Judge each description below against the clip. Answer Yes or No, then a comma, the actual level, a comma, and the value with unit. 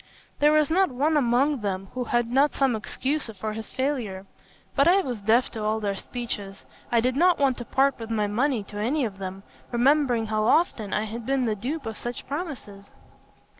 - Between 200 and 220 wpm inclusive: Yes, fast, 205 wpm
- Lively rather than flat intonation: No, average, 4.5 semitones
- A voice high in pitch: Yes, high, 240 Hz